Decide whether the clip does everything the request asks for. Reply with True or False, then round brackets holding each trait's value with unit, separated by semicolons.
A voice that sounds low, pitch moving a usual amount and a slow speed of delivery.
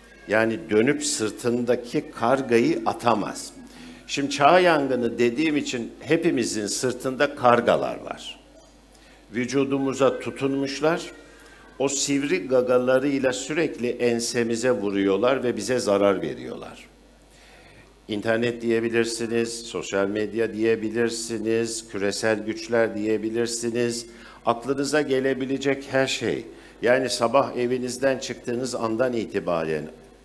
True (120 Hz; 3.1 semitones; 85 wpm)